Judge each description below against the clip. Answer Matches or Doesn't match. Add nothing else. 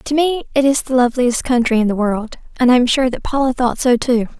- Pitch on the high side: Matches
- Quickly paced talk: Matches